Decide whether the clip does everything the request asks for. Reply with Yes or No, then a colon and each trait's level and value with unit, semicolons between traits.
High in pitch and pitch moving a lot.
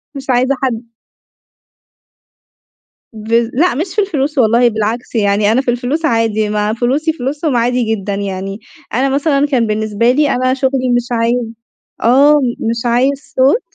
No: high, 245 Hz; average, 3.4 semitones